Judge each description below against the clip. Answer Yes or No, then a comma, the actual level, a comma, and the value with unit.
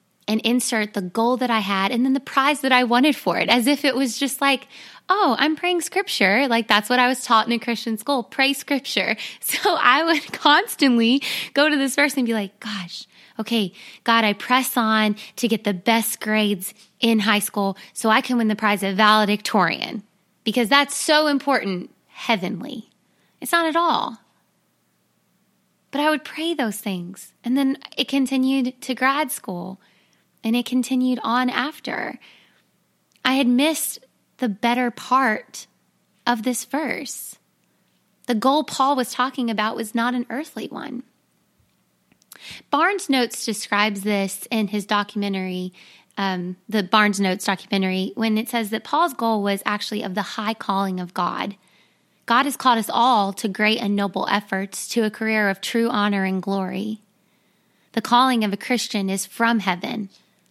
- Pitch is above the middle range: Yes, high, 230 Hz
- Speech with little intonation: No, average, 4.3 semitones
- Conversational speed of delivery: Yes, average, 170 wpm